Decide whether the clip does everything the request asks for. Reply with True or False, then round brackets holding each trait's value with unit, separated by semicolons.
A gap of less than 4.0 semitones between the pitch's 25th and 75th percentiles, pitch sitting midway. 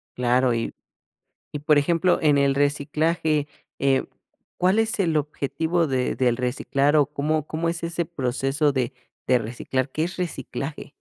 True (3.5 semitones; 145 Hz)